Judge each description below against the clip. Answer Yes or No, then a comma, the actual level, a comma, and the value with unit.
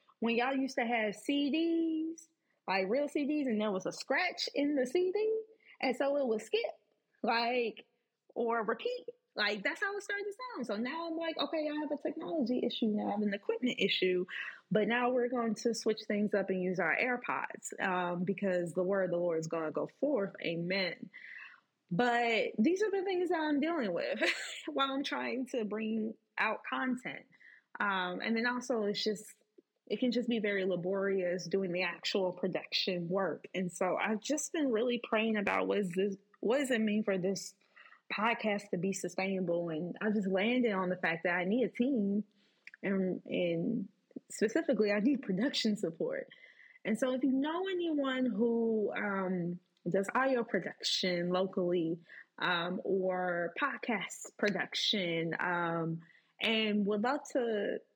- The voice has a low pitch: No, high, 220 Hz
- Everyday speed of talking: Yes, average, 170 wpm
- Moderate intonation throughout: No, wide, 5.9 semitones